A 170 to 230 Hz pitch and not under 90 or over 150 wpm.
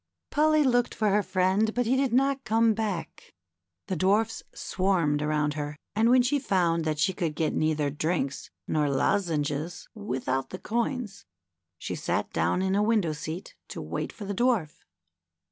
No: high, 190 Hz; average, 165 wpm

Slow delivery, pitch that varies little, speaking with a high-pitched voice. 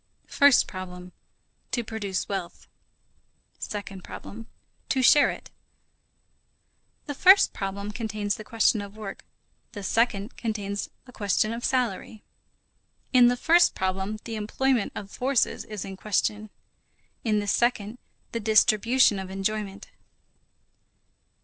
No: slow, 120 wpm; average, 3.1 semitones; high, 215 Hz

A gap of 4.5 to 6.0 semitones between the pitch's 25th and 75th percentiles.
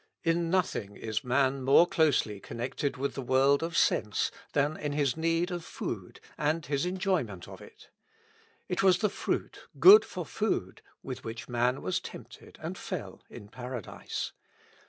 Yes: average, 5.3 semitones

